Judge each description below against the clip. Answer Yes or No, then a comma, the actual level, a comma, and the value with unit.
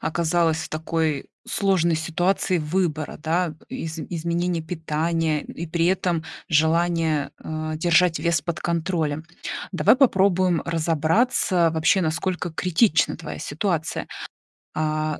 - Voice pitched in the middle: Yes, medium, 165 Hz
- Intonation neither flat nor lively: No, narrow, 2.0 semitones